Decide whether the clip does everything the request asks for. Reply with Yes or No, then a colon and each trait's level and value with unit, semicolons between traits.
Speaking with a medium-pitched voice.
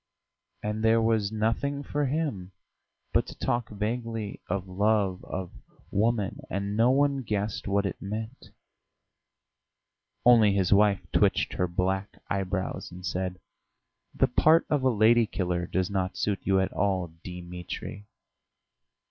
No: low, 100 Hz